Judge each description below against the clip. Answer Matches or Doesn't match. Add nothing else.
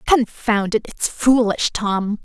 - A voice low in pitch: Doesn't match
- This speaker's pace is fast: Doesn't match